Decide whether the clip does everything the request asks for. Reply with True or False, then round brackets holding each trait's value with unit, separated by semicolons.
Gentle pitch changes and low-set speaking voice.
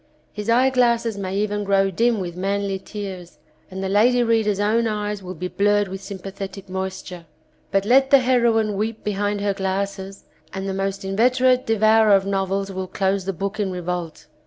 False (2.3 semitones; 200 Hz)